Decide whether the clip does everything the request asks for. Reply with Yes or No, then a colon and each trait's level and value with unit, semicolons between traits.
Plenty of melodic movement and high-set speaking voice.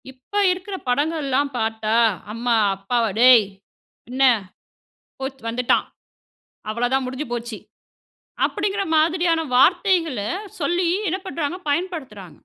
Yes: wide, 6.0 semitones; very high, 270 Hz